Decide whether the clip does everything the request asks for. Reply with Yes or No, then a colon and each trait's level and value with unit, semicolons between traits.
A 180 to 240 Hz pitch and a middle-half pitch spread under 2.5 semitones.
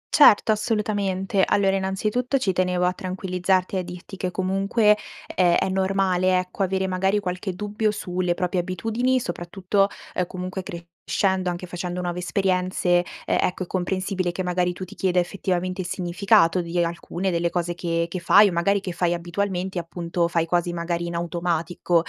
Yes: medium, 185 Hz; narrow, 1.7 semitones